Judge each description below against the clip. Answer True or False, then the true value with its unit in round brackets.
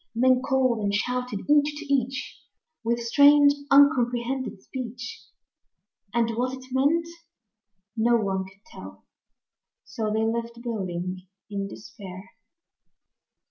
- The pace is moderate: False (110 wpm)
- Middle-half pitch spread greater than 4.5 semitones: False (4.1 semitones)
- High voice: True (235 Hz)